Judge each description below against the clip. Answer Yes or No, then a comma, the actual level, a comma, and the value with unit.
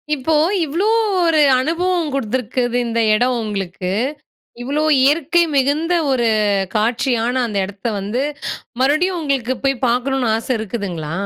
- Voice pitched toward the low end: No, very high, 255 Hz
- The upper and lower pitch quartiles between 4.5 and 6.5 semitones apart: Yes, average, 4.8 semitones